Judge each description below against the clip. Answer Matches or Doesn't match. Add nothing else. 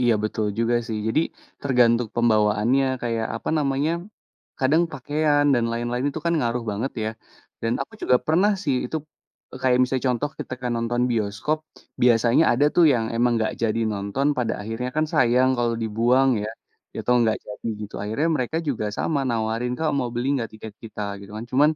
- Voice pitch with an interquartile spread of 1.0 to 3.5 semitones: Matches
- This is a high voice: Doesn't match